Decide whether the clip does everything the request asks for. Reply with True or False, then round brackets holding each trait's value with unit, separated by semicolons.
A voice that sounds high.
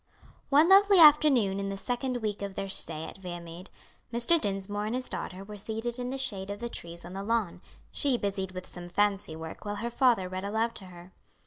True (205 Hz)